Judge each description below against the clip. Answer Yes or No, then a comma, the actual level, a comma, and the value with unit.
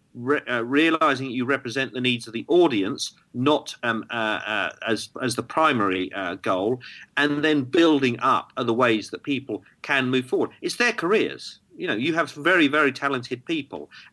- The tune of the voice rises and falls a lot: No, average, 4.1 semitones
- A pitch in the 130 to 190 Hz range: Yes, medium, 140 Hz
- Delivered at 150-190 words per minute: Yes, average, 175 wpm